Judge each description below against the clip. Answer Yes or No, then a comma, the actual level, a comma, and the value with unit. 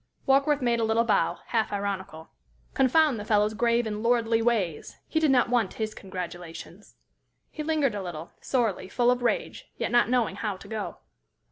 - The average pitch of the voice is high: Yes, high, 225 Hz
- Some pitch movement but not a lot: Yes, average, 3.4 semitones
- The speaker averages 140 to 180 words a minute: Yes, average, 175 wpm